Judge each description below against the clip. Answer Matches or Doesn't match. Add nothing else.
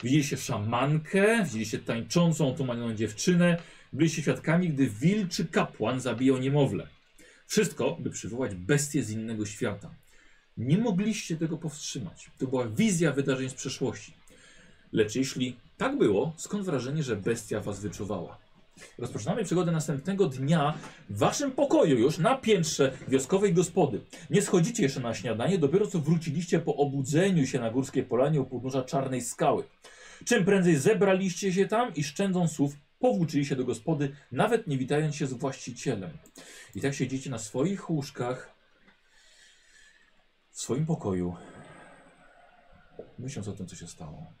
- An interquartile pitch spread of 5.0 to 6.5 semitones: Matches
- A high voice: Doesn't match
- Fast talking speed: Doesn't match